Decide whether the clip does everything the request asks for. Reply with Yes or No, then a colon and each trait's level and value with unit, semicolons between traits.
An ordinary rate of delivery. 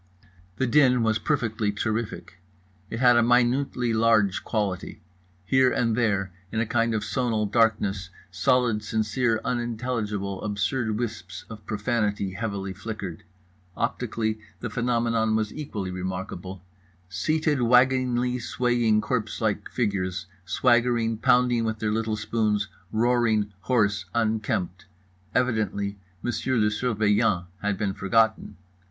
No: slow, 115 wpm